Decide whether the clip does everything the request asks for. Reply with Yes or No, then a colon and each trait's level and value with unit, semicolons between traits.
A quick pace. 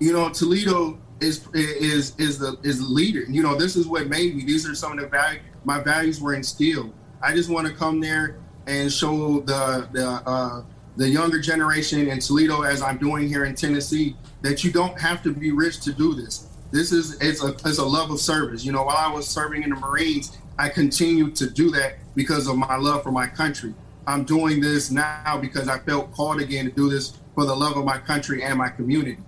Yes: fast, 225 wpm